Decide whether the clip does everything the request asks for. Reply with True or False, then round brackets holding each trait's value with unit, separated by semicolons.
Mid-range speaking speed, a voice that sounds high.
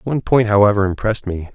False (195 wpm; 105 Hz)